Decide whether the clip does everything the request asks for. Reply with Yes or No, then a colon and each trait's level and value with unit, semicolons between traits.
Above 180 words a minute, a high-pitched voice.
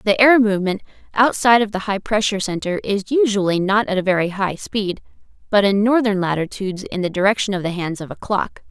Yes: fast, 205 wpm; high, 200 Hz